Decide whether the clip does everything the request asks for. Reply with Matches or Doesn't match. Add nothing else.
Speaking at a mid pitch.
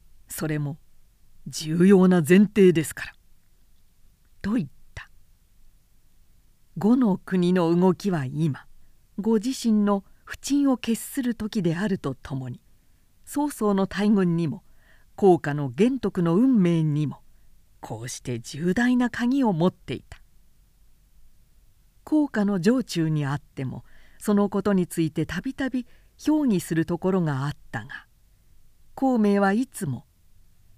Matches